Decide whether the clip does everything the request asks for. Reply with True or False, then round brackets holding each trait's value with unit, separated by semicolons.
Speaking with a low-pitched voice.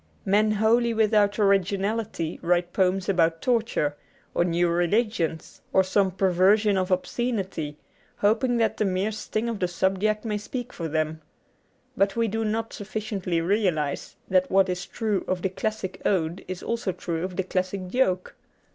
False (195 Hz)